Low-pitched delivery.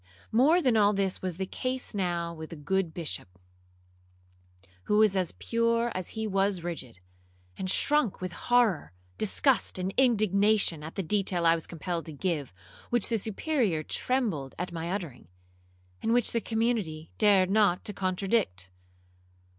No: high, 195 Hz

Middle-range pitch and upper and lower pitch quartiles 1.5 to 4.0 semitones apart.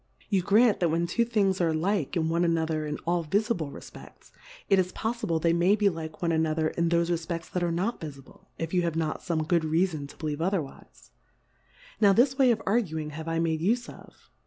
Yes: medium, 170 Hz; average, 3.6 semitones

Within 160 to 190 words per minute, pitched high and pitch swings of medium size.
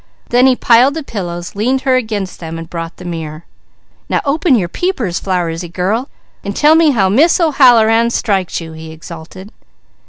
No: average, 175 wpm; high, 205 Hz; wide, 7.0 semitones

